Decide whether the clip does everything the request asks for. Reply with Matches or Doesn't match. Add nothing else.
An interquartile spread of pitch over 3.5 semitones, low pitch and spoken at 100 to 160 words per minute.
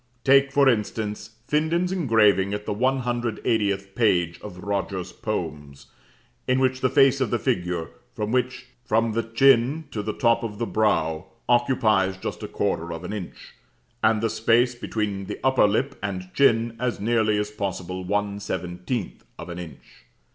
Matches